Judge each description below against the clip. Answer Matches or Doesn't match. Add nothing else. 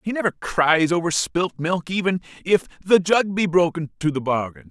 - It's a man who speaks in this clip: Matches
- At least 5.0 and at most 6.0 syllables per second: Doesn't match